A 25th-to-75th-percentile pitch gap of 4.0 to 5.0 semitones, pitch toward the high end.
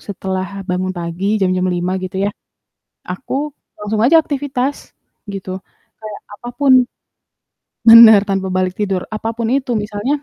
Yes: average, 4.4 semitones; high, 205 Hz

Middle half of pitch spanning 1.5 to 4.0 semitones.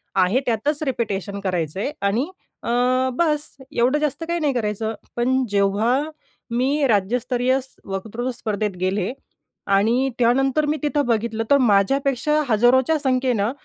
No: average, 4.5 semitones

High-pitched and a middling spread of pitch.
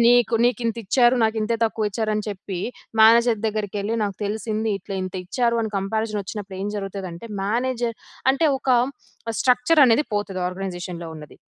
Yes: high, 215 Hz; average, 3.0 semitones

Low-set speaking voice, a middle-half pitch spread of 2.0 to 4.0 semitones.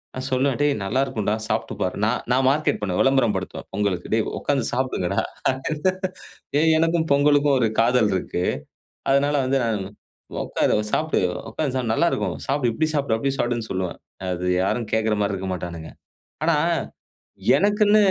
No: low, 125 Hz; wide, 5.4 semitones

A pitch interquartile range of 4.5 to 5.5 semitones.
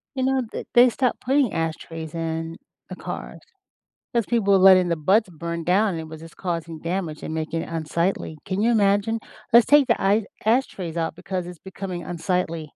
Yes: average, 4.8 semitones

